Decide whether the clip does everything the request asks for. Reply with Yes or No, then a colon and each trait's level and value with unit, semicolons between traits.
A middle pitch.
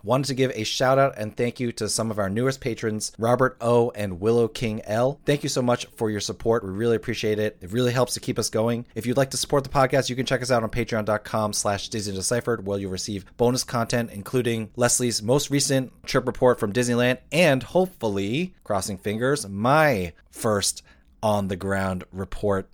No: low, 115 Hz